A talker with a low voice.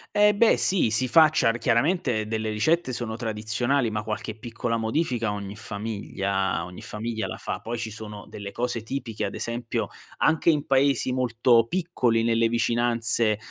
Yes: low, 115 Hz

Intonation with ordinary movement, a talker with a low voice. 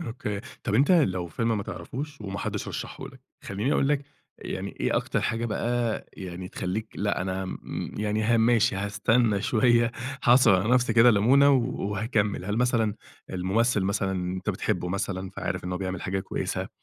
Yes: average, 3.6 semitones; low, 105 Hz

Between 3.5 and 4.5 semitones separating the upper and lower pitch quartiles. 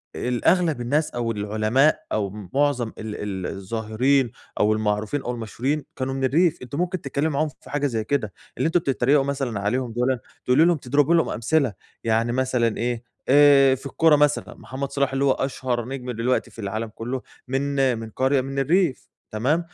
Yes: average, 3.8 semitones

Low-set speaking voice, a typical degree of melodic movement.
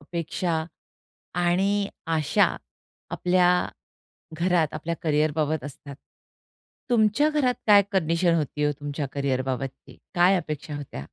No: medium, 160 Hz; average, 3.9 semitones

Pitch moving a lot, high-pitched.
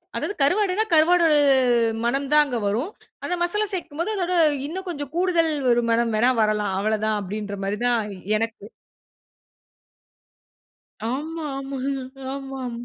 Yes: wide, 7.0 semitones; very high, 275 Hz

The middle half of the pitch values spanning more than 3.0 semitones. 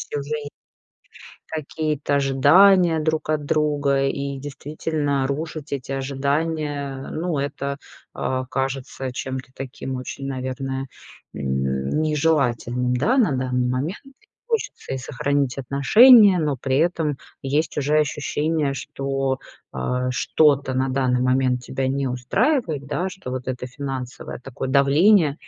No: average, 2.7 semitones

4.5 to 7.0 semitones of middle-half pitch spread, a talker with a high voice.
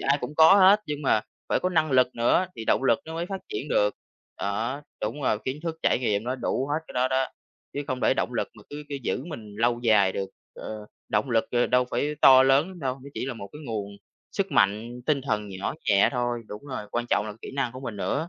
No: average, 4.8 semitones; low, 125 Hz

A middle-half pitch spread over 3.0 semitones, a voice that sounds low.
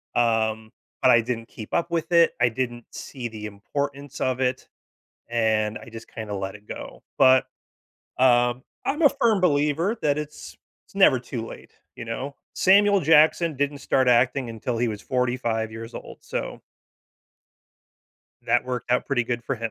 Yes: average, 4.0 semitones; low, 125 Hz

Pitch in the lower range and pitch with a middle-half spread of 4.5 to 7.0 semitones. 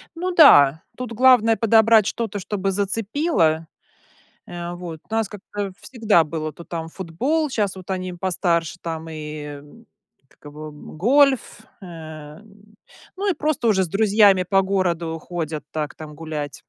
No: high, 190 Hz; wide, 5.5 semitones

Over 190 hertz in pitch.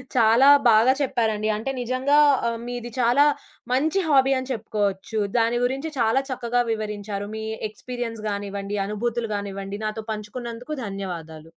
Yes: high, 225 Hz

